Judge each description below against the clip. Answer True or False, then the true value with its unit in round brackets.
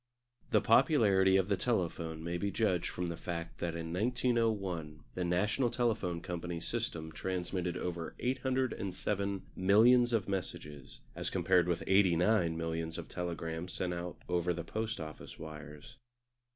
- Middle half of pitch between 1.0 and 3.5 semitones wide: False (4.2 semitones)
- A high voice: False (90 Hz)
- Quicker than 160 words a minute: False (140 wpm)